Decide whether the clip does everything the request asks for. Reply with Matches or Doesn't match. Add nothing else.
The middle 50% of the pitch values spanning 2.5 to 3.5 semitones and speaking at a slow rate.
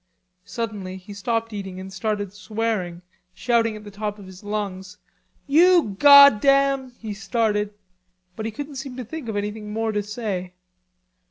Doesn't match